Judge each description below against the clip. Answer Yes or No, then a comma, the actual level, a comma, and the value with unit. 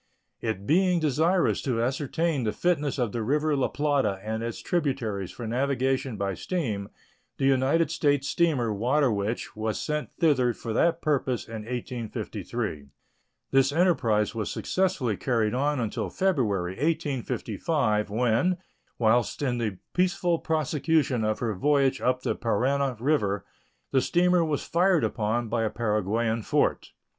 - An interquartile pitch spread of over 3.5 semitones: Yes, average, 5.3 semitones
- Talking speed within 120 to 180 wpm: Yes, average, 140 wpm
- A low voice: Yes, low, 130 Hz